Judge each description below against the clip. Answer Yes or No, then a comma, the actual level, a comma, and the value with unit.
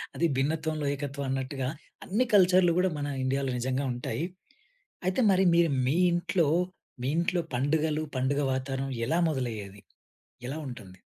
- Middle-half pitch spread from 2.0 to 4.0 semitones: No, average, 4.5 semitones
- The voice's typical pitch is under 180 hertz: Yes, medium, 140 Hz